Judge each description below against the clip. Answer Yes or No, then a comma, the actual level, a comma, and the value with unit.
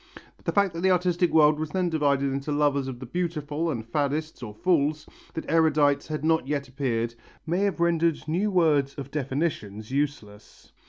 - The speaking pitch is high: No, medium, 150 Hz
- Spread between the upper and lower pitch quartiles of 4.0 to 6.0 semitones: No, average, 3.2 semitones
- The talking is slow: No, average, 175 wpm